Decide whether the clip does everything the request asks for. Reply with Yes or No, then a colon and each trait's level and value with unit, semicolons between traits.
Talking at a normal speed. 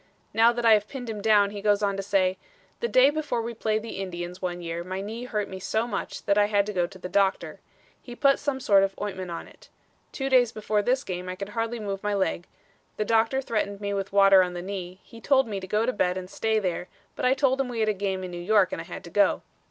No: fast, 270 wpm